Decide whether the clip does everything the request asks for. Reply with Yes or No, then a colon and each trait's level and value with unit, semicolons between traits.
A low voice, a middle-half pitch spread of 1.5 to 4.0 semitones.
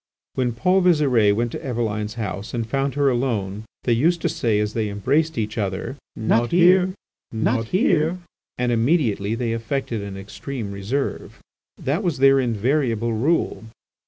No: low, 120 Hz; average, 4.7 semitones